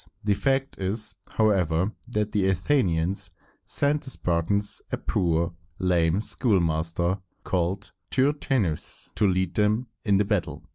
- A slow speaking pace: Yes, slow, 125 wpm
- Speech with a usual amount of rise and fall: Yes, average, 3.9 semitones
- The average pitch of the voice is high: No, low, 100 Hz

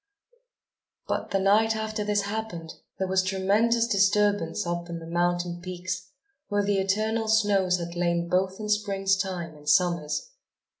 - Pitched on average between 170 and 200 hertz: Yes, high, 190 Hz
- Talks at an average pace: Yes, average, 150 wpm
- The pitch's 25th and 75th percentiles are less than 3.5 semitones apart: Yes, average, 3.0 semitones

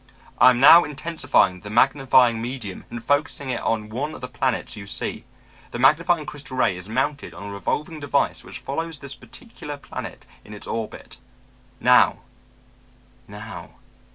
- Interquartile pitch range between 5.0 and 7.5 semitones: No, average, 4.5 semitones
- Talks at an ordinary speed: Yes, average, 155 wpm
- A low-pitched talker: Yes, low, 130 Hz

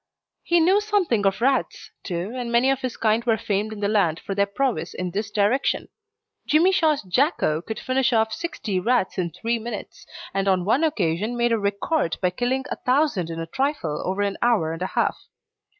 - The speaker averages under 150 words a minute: No, average, 200 wpm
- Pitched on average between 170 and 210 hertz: No, high, 220 Hz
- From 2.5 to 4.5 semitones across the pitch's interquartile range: No, average, 5.3 semitones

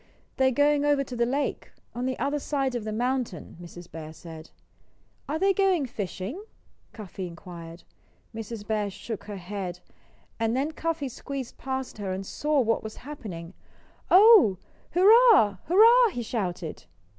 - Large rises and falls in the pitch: Yes, wide, 7.2 semitones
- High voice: Yes, high, 240 Hz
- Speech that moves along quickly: No, average, 155 wpm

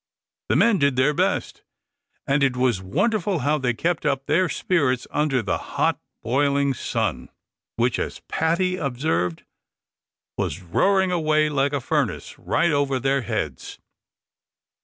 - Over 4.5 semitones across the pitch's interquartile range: No, average, 4.2 semitones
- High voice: No, medium, 140 Hz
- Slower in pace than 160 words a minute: Yes, average, 140 wpm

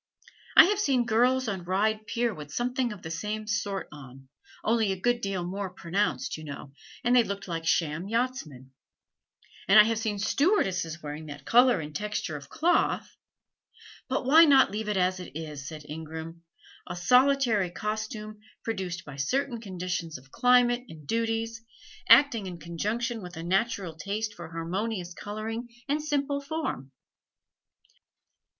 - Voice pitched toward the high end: Yes, high, 205 Hz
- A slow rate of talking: No, average, 155 wpm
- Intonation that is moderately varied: No, wide, 6.1 semitones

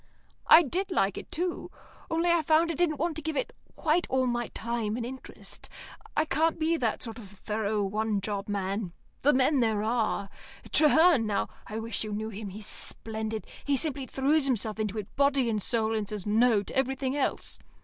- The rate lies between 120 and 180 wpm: No, average, 195 wpm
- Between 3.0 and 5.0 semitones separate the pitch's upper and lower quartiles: No, wide, 5.6 semitones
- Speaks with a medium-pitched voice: No, high, 235 Hz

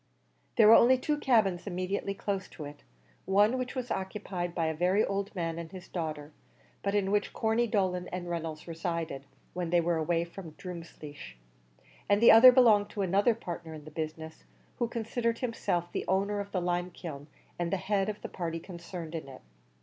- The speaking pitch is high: No, medium, 180 Hz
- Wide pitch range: No, average, 3.7 semitones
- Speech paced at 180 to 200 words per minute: Yes, average, 190 wpm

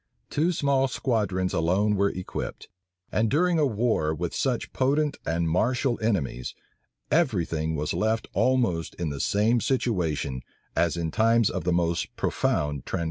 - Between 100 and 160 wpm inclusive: Yes, average, 150 wpm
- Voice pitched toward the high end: No, low, 100 Hz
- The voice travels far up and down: Yes, wide, 7.2 semitones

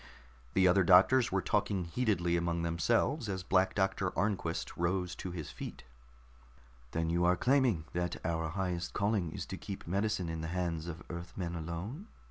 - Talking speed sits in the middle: Yes, average, 165 wpm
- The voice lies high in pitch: No, very low, 90 Hz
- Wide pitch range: No, average, 2.7 semitones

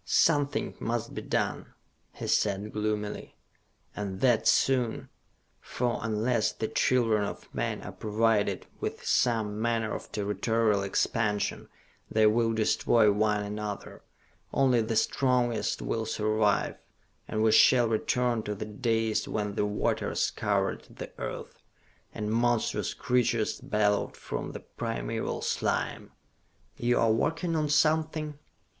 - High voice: No, low, 110 Hz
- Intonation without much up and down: Yes, narrow, 2.3 semitones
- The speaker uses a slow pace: Yes, slow, 125 wpm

